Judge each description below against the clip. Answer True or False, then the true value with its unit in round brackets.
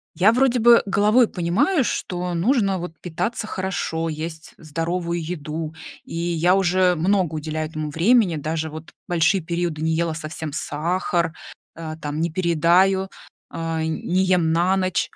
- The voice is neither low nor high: True (170 Hz)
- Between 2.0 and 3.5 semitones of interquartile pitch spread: True (2.7 semitones)